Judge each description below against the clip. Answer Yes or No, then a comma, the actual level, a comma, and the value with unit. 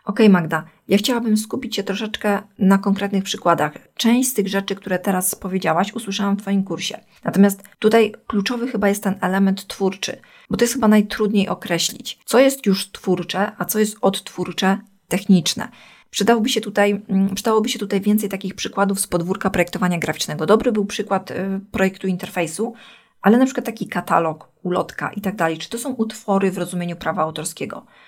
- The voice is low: No, high, 200 Hz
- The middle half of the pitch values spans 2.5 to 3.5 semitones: Yes, average, 2.8 semitones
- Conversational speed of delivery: No, fast, 165 wpm